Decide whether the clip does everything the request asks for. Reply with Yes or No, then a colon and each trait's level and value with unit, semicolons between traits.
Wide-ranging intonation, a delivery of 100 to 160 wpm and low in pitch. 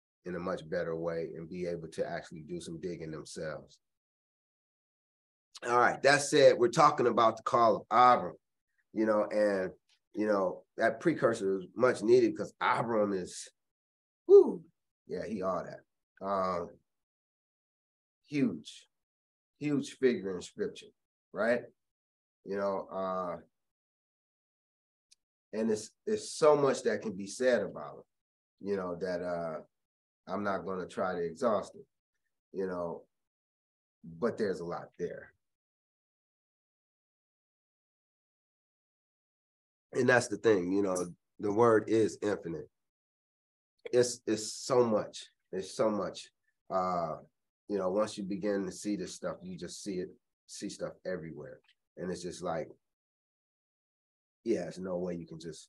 Yes: wide, 6.2 semitones; slow, 135 wpm; low, 100 Hz